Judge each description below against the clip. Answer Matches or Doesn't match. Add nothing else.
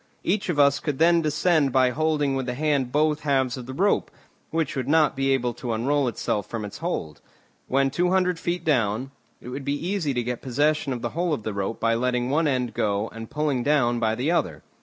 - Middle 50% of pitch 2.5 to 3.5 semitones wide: Doesn't match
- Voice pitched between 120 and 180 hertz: Matches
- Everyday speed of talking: Doesn't match